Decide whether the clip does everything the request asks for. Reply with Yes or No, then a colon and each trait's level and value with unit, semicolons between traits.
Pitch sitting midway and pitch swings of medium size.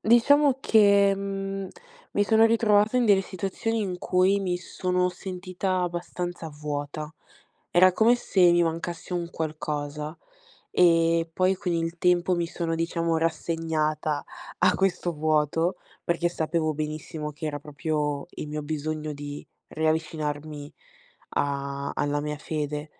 Yes: medium, 165 Hz; average, 3.4 semitones